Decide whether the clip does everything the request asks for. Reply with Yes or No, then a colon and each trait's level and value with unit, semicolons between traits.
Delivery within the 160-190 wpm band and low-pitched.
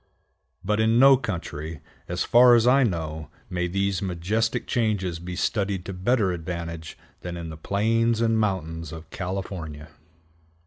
No: average, 145 wpm; very low, 95 Hz